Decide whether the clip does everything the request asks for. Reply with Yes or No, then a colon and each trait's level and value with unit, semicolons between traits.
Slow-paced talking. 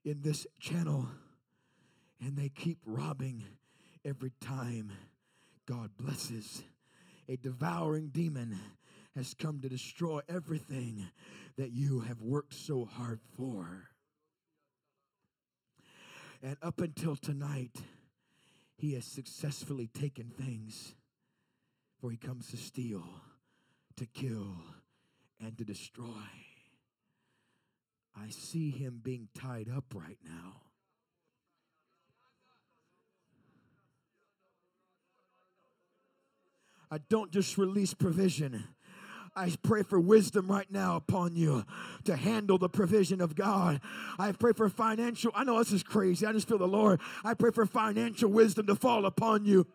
Yes: slow, 115 wpm